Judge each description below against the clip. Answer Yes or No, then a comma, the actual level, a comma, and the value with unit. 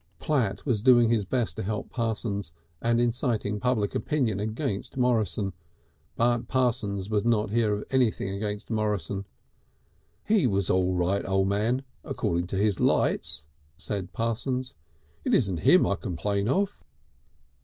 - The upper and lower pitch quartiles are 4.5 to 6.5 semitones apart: No, average, 3.5 semitones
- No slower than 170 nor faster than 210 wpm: No, average, 140 wpm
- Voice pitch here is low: Yes, low, 110 Hz